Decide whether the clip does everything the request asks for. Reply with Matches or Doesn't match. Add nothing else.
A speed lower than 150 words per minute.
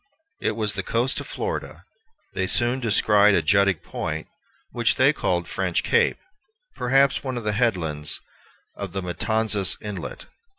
Matches